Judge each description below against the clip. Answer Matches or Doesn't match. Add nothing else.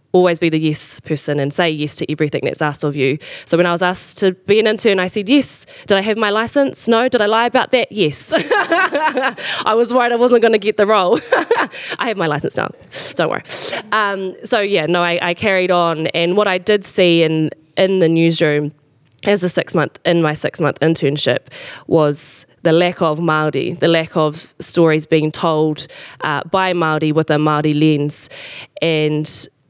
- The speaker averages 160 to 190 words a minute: Doesn't match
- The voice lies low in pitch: Doesn't match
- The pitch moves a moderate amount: Matches